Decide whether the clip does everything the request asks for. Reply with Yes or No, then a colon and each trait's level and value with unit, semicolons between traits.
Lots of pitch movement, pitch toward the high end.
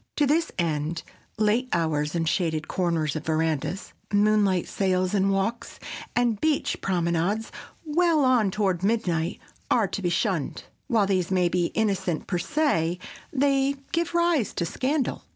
Yes: wide, 6.2 semitones; high, 195 Hz